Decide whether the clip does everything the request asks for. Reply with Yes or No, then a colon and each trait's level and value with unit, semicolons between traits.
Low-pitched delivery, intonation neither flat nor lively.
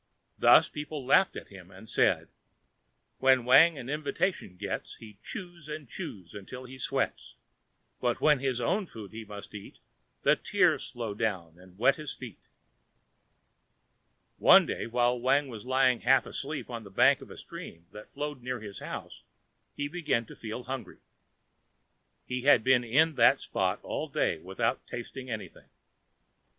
Yes: low, 125 Hz; average, 4.2 semitones